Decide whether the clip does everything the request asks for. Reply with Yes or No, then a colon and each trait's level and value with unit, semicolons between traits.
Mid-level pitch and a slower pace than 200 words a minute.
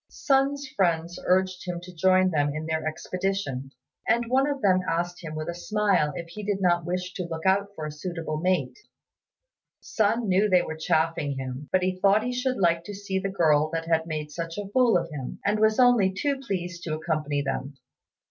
No: medium, 180 Hz; fast, 205 wpm